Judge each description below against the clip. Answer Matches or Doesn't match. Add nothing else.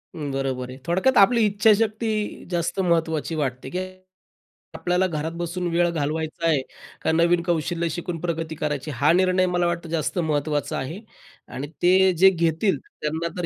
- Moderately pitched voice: Matches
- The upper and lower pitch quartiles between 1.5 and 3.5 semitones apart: Matches